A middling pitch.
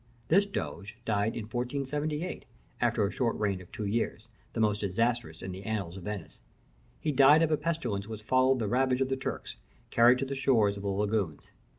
No: low, 115 Hz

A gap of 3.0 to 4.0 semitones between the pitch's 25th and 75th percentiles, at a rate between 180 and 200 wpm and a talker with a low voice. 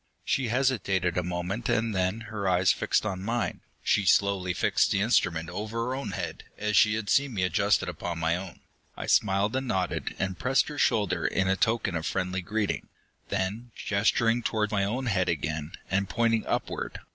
Yes: average, 3.6 semitones; average, 185 wpm; low, 100 Hz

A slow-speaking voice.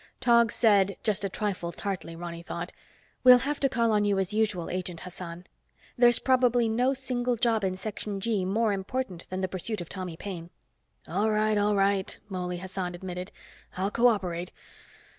No: average, 175 wpm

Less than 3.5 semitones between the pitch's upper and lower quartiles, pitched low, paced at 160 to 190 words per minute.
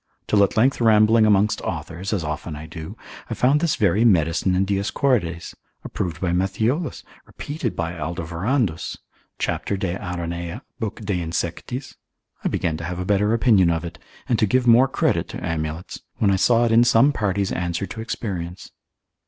No: average, 5.0 semitones; very low, 95 Hz; average, 170 wpm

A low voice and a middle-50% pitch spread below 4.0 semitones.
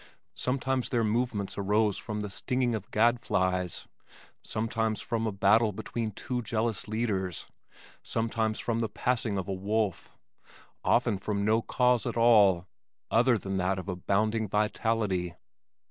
Yes: low, 110 Hz; average, 2.8 semitones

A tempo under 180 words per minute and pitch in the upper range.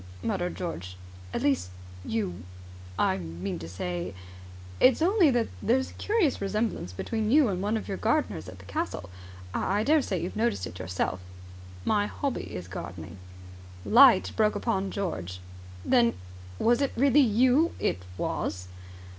Yes: average, 155 wpm; high, 195 Hz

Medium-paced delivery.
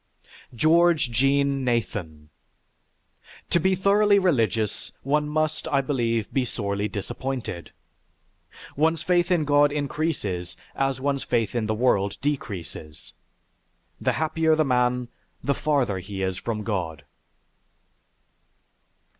No: slow, 115 wpm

